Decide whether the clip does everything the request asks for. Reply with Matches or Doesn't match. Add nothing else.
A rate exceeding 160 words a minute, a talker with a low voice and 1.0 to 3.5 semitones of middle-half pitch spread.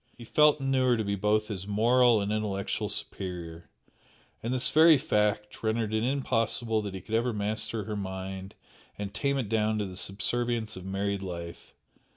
Matches